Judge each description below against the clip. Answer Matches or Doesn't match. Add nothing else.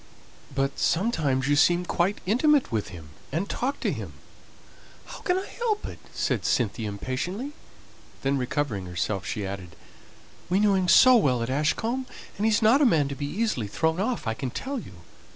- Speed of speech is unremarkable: Matches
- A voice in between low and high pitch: Matches